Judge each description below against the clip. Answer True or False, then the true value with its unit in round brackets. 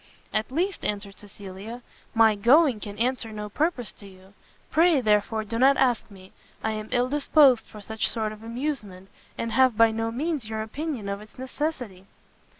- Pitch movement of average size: True (3.9 semitones)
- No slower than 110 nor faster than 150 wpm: False (175 wpm)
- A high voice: True (225 Hz)